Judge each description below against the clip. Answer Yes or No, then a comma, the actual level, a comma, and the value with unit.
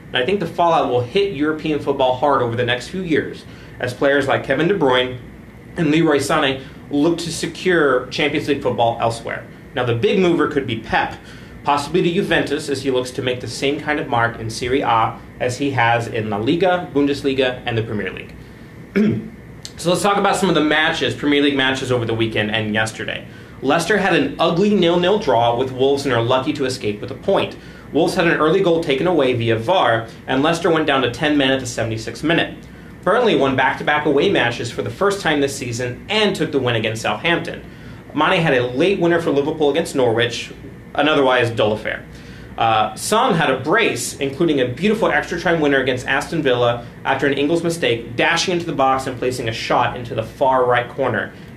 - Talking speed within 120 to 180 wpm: No, fast, 205 wpm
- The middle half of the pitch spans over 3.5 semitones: Yes, average, 4.7 semitones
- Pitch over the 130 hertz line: Yes, medium, 140 Hz